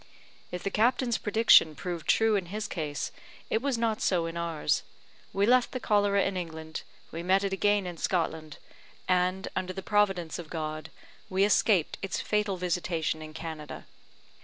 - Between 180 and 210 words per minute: No, average, 165 wpm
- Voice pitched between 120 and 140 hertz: No, medium, 185 Hz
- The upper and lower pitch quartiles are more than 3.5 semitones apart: Yes, average, 3.9 semitones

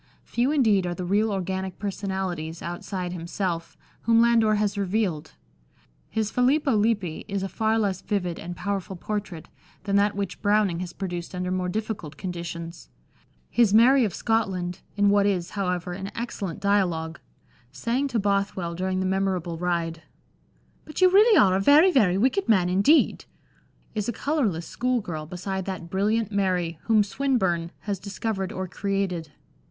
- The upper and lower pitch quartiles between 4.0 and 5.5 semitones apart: No, average, 3.4 semitones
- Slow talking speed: No, average, 160 wpm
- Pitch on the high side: Yes, high, 195 Hz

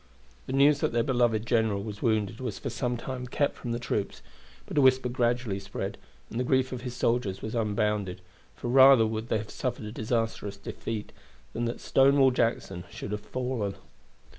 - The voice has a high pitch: No, low, 115 Hz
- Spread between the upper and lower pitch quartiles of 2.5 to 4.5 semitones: Yes, average, 3.0 semitones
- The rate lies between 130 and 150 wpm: No, average, 190 wpm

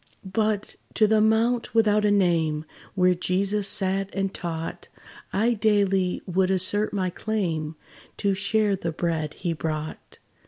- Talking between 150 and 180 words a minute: No, average, 140 wpm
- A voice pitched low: No, high, 195 Hz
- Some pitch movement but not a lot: Yes, average, 3.4 semitones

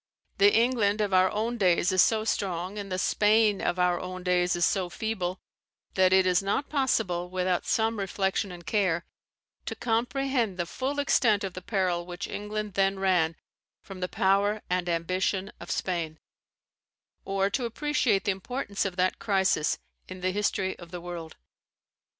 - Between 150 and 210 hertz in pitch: Yes, high, 190 Hz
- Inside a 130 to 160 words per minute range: No, average, 170 wpm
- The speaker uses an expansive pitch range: No, average, 2.7 semitones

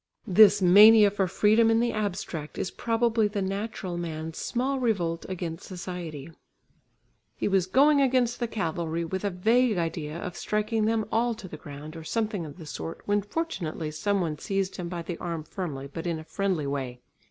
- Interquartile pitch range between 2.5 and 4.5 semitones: No, average, 4.9 semitones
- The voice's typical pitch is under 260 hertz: Yes, high, 190 Hz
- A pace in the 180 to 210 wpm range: Yes, average, 185 wpm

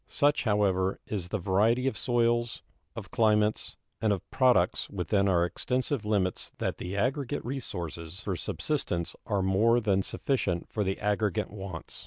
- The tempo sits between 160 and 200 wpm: No, average, 150 wpm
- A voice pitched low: Yes, low, 105 Hz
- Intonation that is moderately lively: Yes, average, 3.9 semitones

